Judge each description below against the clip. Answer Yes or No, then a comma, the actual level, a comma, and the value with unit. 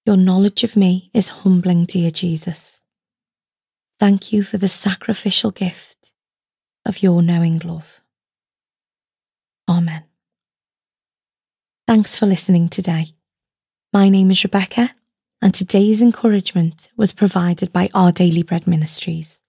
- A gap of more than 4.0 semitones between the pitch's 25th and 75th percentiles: No, average, 2.9 semitones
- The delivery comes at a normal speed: No, slow, 115 wpm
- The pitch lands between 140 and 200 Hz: Yes, high, 190 Hz